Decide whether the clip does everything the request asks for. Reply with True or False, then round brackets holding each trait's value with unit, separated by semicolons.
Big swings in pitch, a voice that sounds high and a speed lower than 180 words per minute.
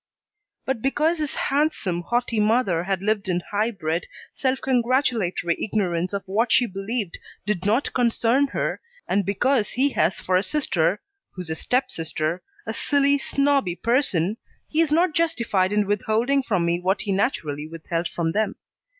True (6.4 semitones; 210 Hz; 160 wpm)